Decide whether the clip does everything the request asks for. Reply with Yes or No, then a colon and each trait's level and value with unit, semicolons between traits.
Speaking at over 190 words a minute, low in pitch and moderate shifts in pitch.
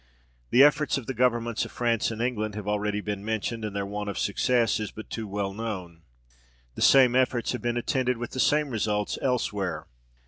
Yes: average, 200 wpm; low, 110 Hz; average, 3.1 semitones